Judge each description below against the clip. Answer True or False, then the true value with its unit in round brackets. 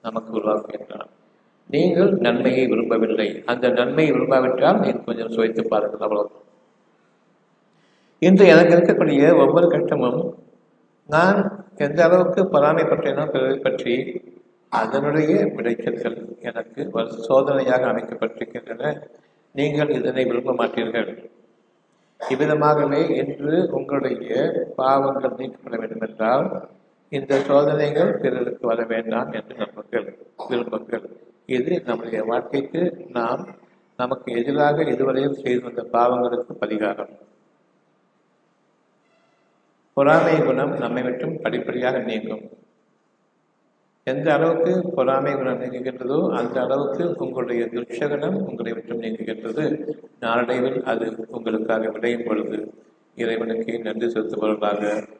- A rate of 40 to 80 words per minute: False (90 wpm)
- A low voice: True (125 Hz)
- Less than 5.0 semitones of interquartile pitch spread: True (4.4 semitones)